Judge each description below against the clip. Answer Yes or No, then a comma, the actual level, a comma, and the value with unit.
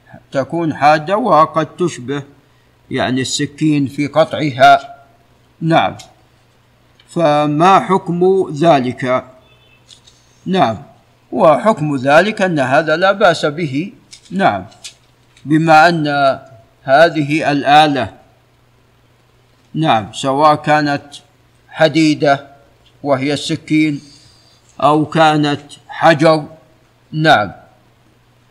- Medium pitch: Yes, medium, 145 Hz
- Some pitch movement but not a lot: Yes, average, 3.5 semitones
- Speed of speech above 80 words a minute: No, average, 75 wpm